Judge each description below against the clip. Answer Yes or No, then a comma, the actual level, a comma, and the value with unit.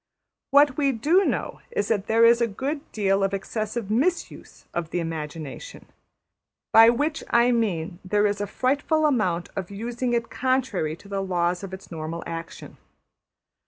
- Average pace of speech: Yes, average, 170 wpm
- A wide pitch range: Yes, wide, 5.9 semitones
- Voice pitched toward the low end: No, high, 215 Hz